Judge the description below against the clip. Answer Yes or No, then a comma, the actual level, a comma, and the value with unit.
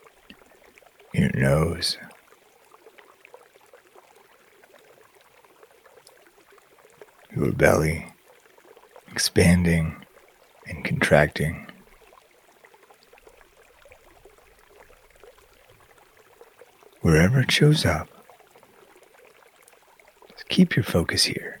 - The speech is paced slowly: Yes, slow, 40 wpm